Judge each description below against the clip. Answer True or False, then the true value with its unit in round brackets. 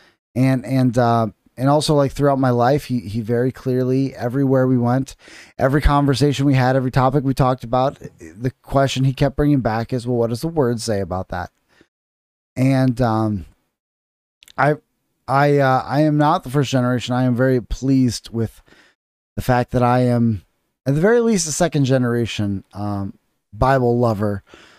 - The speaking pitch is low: True (125 Hz)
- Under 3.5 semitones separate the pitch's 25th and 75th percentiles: True (2.9 semitones)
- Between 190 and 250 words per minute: False (170 wpm)